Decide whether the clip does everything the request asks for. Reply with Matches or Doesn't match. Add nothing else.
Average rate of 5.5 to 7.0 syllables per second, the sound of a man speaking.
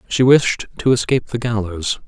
Doesn't match